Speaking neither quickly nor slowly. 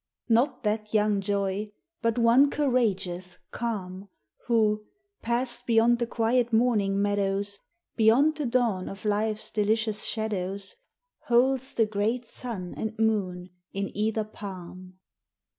No: slow, 120 wpm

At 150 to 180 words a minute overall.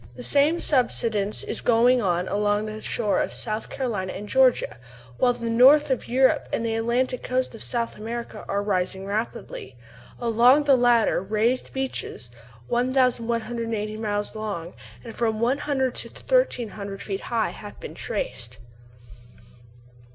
No: average, 140 wpm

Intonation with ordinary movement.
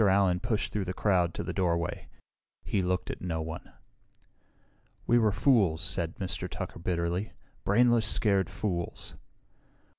Yes: average, 3.2 semitones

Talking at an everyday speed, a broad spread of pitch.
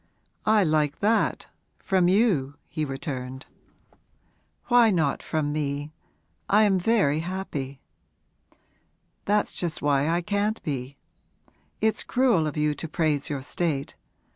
No: slow, 120 wpm; wide, 6.0 semitones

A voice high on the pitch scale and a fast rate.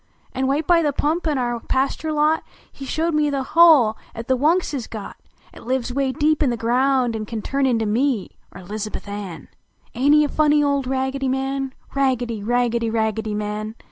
No: very high, 260 Hz; average, 195 wpm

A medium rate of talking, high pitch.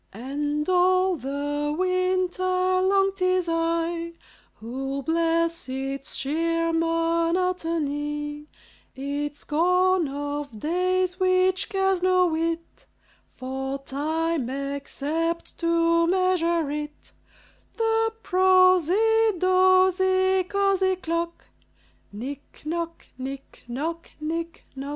No: slow, 90 wpm; very high, 335 Hz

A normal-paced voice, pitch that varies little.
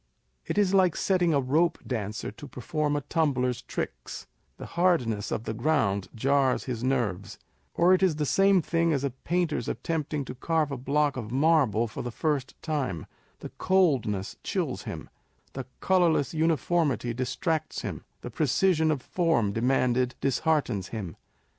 No: average, 160 wpm; average, 5.1 semitones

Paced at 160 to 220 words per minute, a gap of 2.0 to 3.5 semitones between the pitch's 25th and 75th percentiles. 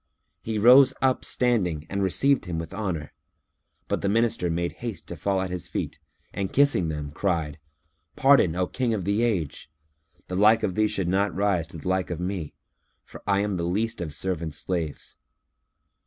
No: average, 185 wpm; average, 4.1 semitones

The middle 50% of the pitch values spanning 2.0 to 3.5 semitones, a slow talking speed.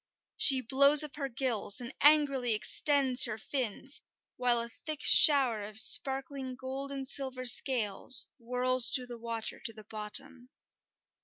No: average, 2.8 semitones; average, 145 wpm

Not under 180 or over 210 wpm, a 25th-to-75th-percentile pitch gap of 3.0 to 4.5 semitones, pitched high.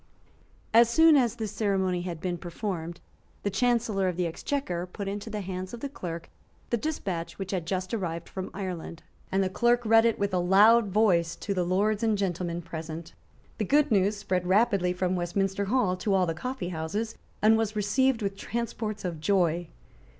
Yes: average, 185 wpm; average, 3.7 semitones; high, 195 Hz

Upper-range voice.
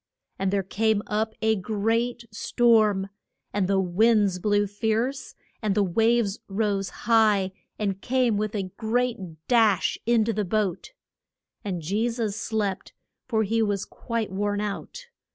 Yes: high, 215 Hz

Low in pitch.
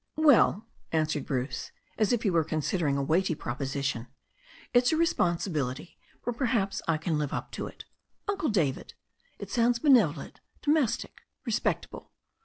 No: medium, 175 Hz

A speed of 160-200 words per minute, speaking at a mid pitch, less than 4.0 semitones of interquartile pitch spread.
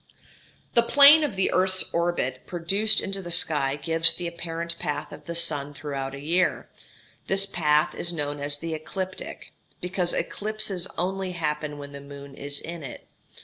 No: average, 165 wpm; medium, 170 Hz; average, 4.3 semitones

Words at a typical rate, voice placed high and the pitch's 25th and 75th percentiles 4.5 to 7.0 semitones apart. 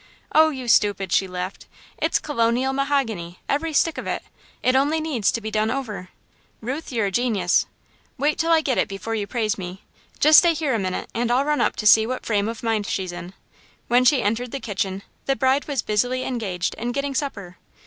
No: fast, 210 wpm; high, 235 Hz; average, 5.2 semitones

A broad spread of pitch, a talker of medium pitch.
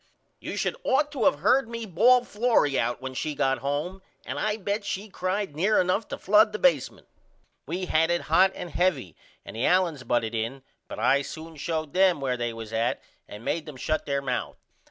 Yes: wide, 7.1 semitones; medium, 165 Hz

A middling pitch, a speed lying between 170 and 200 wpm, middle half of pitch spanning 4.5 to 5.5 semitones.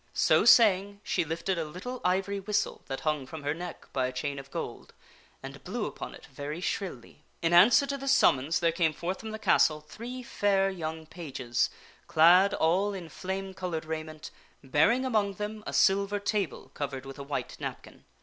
Yes: medium, 175 Hz; average, 185 wpm; average, 4.8 semitones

